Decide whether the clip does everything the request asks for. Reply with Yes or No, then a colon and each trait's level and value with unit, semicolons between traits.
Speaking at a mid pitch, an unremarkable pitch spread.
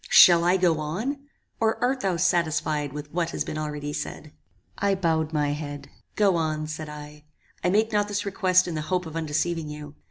Yes: medium, 160 Hz; average, 3.6 semitones